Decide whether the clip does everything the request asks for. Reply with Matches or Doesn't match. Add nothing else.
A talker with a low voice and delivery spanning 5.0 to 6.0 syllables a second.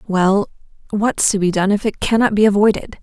Doesn't match